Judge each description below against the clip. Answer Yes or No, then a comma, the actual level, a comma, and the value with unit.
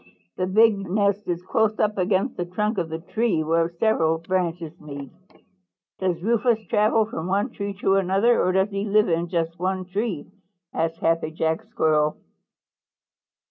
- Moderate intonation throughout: Yes, average, 4.1 semitones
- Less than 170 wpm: Yes, average, 160 wpm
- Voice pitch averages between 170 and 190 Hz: Yes, medium, 185 Hz